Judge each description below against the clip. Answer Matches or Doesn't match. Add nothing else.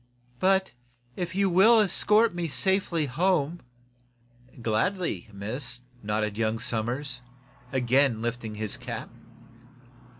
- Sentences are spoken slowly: Matches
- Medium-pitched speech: Doesn't match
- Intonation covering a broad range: Matches